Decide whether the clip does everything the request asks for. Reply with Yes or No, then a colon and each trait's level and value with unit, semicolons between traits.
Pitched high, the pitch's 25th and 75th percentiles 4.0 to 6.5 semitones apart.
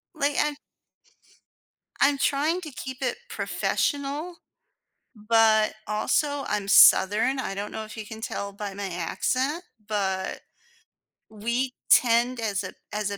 Yes: high, 225 Hz; average, 5.1 semitones